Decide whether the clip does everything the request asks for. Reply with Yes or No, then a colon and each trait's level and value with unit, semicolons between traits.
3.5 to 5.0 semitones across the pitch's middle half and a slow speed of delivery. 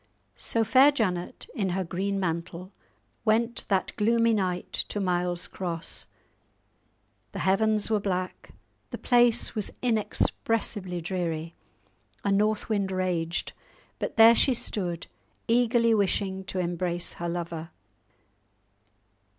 Yes: average, 3.9 semitones; slow, 115 wpm